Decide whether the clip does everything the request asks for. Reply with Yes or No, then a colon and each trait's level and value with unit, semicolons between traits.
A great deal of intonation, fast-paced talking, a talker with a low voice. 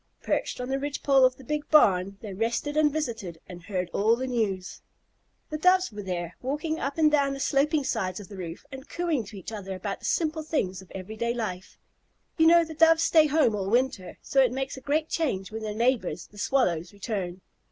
No: wide, 7.4 semitones; fast, 225 wpm; high, 240 Hz